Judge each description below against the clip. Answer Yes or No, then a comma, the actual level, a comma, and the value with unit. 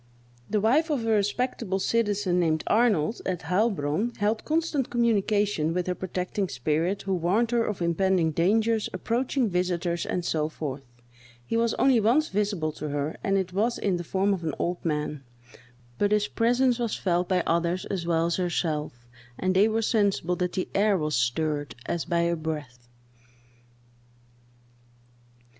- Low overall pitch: No, medium, 185 Hz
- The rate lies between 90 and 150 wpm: No, average, 160 wpm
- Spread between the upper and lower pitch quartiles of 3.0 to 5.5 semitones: Yes, average, 4.7 semitones